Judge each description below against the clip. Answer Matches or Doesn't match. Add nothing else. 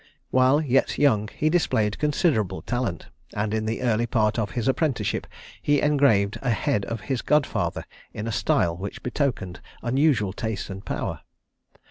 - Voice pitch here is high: Doesn't match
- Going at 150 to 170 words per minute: Matches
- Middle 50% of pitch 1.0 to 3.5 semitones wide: Doesn't match